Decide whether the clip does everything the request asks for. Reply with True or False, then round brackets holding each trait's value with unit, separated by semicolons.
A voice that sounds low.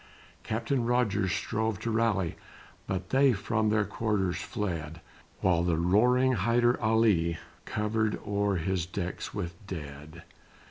True (105 Hz)